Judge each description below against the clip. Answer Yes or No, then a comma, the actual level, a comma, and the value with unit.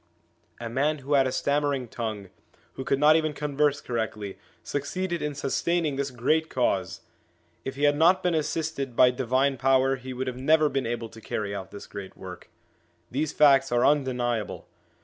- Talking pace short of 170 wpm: No, average, 175 wpm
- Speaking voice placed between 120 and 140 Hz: Yes, low, 135 Hz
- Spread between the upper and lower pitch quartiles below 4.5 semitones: Yes, average, 3.5 semitones